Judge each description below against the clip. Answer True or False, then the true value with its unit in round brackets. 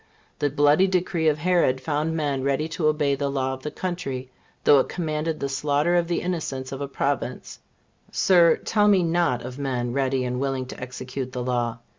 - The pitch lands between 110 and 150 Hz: True (140 Hz)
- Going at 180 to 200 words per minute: True (195 wpm)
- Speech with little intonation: False (3.7 semitones)